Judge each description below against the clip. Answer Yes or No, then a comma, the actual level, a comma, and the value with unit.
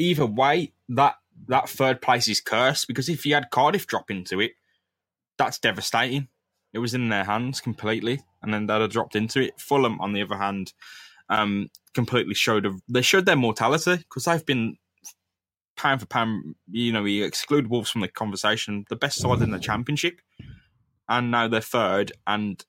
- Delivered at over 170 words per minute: Yes, average, 185 wpm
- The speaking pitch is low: Yes, low, 115 Hz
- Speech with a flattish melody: No, average, 3.8 semitones